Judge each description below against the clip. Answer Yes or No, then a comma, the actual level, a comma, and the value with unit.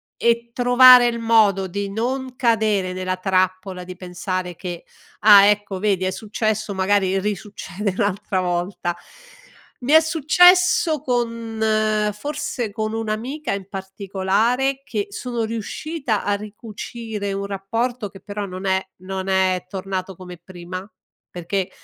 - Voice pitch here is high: Yes, high, 205 Hz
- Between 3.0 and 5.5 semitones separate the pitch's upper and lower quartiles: Yes, average, 3.7 semitones